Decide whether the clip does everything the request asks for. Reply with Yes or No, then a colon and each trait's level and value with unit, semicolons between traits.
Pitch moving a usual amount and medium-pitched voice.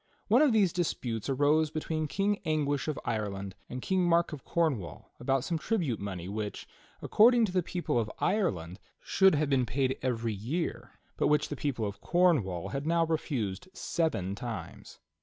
No: wide, 7.4 semitones; medium, 145 Hz